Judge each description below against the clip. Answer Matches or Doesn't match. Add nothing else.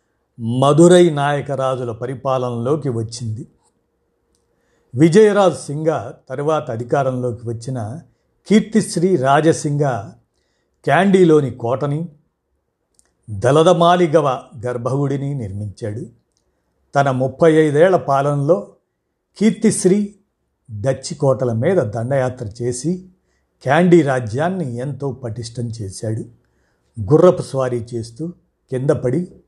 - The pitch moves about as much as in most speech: Doesn't match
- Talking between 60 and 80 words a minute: Matches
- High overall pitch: Doesn't match